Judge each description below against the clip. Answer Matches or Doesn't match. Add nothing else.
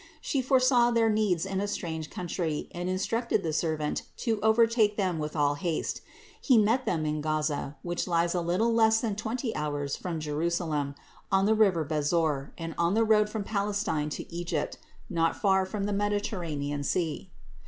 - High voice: Doesn't match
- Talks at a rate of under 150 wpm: Doesn't match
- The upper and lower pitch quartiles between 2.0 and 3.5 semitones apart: Doesn't match